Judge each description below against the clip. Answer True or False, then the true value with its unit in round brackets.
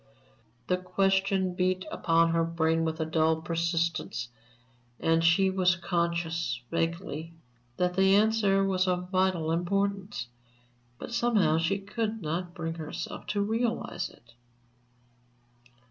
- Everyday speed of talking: False (120 wpm)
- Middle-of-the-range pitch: True (180 Hz)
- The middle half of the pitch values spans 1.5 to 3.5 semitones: True (2.8 semitones)